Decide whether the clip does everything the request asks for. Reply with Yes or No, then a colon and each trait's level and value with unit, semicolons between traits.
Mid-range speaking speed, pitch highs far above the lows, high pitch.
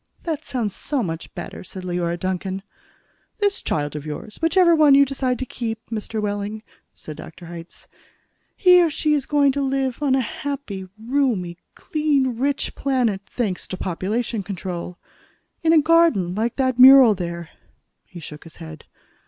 Yes: average, 160 wpm; wide, 7.3 semitones; high, 230 Hz